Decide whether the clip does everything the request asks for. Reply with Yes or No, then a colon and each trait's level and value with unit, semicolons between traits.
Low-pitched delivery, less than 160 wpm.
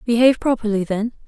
No: high, 225 Hz; average, 140 wpm